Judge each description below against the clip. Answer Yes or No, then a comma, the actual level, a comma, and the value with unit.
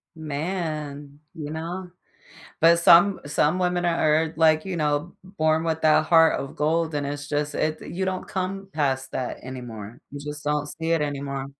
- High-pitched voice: No, medium, 155 Hz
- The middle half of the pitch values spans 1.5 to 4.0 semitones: Yes, narrow, 2.6 semitones